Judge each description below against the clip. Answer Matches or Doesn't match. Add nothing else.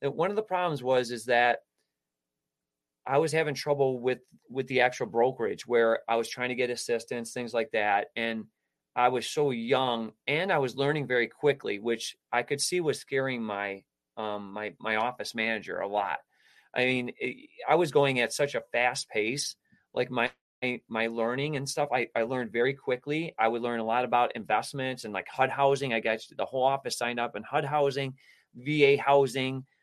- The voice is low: Matches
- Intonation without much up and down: Doesn't match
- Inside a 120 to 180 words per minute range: Doesn't match